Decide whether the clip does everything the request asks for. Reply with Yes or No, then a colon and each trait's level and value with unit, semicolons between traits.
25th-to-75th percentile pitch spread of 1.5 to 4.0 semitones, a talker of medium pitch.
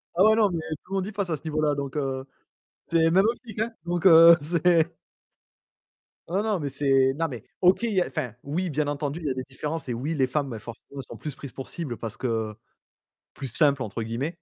No: average, 4.7 semitones; medium, 150 Hz